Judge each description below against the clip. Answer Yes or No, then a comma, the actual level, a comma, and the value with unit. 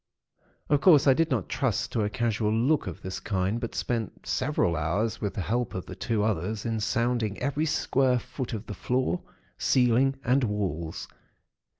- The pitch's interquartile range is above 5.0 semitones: No, average, 4.0 semitones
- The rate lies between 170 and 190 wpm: Yes, average, 180 wpm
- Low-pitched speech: Yes, low, 115 Hz